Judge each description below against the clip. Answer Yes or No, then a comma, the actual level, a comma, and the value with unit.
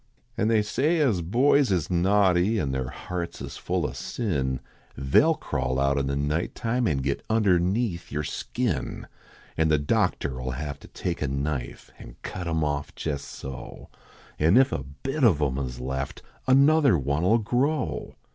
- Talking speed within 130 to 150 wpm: No, average, 175 wpm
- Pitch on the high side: No, very low, 85 Hz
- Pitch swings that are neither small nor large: No, wide, 8.3 semitones